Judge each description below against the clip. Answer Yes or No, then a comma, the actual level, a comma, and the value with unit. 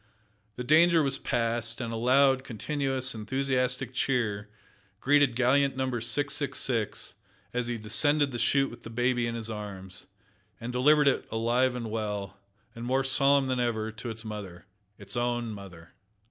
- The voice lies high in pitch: No, low, 120 Hz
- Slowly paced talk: No, average, 155 wpm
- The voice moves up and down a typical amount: Yes, average, 3.0 semitones